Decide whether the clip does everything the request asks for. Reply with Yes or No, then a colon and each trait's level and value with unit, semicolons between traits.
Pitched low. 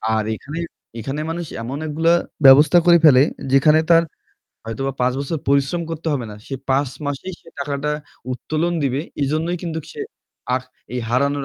No: medium, 145 Hz